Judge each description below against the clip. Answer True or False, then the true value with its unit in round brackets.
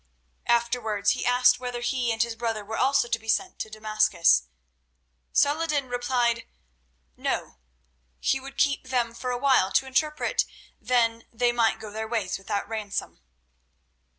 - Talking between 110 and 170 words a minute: True (145 wpm)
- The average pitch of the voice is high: True (235 Hz)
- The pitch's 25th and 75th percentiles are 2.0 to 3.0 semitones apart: True (2.5 semitones)